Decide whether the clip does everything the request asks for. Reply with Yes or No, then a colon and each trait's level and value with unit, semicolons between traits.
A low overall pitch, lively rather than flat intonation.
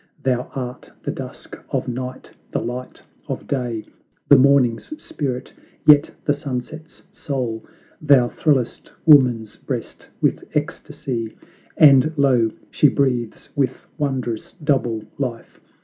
No: low, 130 Hz; average, 2.8 semitones